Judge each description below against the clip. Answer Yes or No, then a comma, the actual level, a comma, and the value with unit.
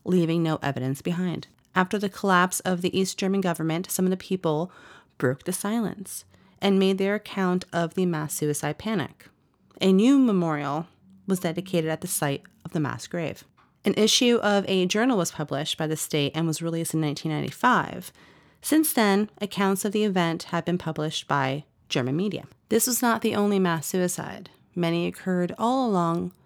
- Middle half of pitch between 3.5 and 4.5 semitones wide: Yes, average, 3.8 semitones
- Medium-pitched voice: Yes, medium, 180 Hz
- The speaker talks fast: No, average, 175 wpm